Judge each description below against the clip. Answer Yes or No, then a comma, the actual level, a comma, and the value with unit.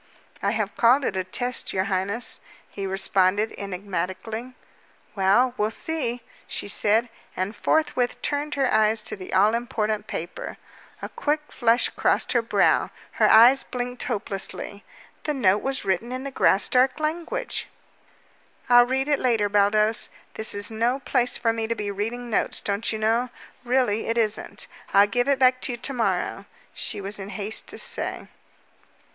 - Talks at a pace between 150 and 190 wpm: Yes, average, 165 wpm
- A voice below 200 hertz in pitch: No, high, 225 Hz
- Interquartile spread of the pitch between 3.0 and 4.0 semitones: Yes, average, 3.6 semitones